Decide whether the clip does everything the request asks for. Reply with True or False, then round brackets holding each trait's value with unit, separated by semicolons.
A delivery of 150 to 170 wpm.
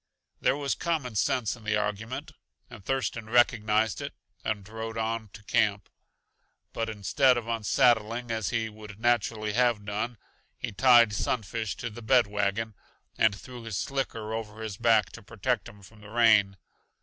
True (160 wpm)